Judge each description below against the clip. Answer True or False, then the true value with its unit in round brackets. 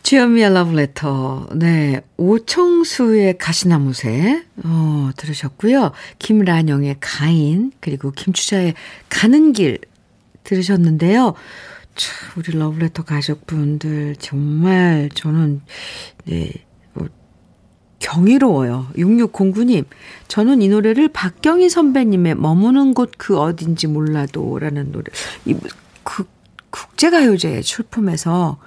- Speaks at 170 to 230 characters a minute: True (225 characters per minute)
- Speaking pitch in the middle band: True (170 Hz)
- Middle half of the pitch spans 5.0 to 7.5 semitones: True (6.6 semitones)